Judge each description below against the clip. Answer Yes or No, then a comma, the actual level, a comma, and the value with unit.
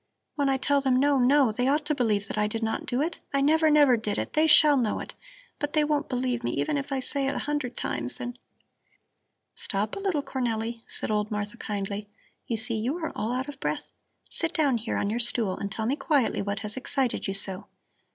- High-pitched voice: Yes, very high, 250 Hz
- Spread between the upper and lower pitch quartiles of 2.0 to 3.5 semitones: No, average, 4.9 semitones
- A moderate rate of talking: No, fast, 235 wpm